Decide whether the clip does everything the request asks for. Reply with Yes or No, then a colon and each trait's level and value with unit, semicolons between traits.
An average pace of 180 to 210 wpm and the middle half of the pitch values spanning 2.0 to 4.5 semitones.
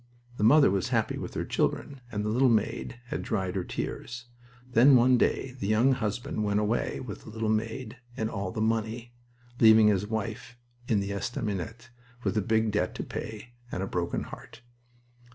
Yes: average, 185 wpm; narrow, 2.5 semitones